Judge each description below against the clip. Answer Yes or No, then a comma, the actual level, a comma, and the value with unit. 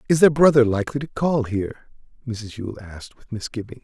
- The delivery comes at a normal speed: Yes, average, 190 wpm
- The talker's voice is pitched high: No, low, 120 Hz